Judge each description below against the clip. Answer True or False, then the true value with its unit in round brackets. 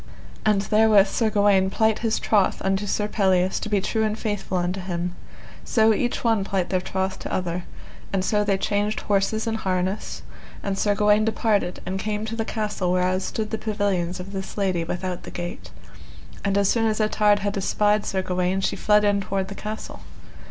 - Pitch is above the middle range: True (200 Hz)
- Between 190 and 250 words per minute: True (195 wpm)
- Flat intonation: True (2.1 semitones)